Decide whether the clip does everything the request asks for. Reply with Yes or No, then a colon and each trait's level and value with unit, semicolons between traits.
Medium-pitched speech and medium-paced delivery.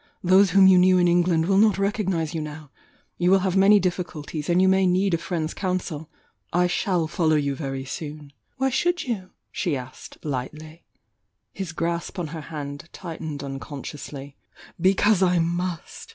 Yes: medium, 175 Hz; average, 175 wpm